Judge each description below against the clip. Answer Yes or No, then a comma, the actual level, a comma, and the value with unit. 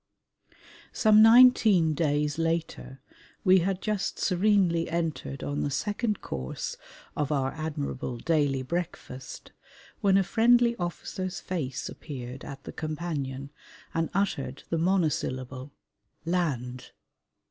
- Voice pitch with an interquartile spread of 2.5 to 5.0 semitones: No, wide, 5.4 semitones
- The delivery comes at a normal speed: No, slow, 110 wpm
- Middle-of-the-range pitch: Yes, medium, 165 Hz